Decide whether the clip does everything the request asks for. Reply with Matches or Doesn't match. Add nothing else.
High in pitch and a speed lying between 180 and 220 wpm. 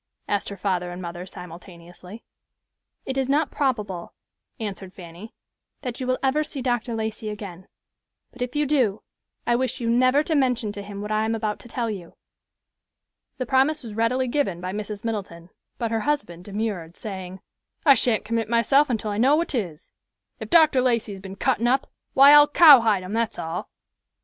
Matches